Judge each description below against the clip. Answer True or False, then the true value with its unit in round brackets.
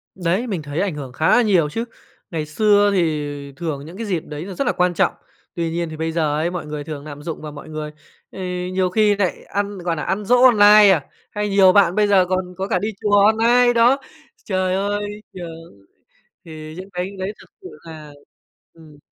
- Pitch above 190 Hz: False (185 Hz)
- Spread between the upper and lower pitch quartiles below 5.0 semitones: True (4.5 semitones)